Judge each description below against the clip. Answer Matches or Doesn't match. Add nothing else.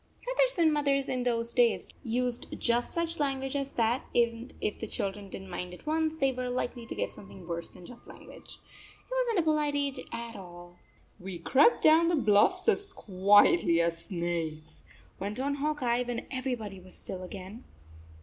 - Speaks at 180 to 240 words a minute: Matches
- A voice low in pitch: Doesn't match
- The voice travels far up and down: Matches